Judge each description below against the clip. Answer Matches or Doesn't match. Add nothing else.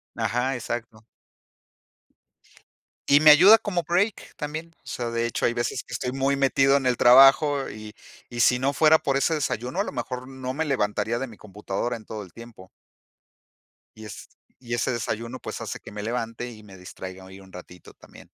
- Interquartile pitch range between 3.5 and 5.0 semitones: Matches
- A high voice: Doesn't match